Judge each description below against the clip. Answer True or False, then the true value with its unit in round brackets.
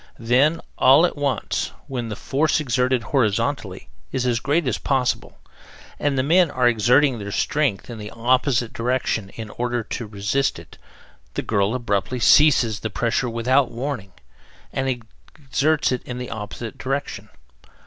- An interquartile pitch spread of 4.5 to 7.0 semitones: False (3.3 semitones)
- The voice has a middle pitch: False (125 Hz)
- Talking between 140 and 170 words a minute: True (150 wpm)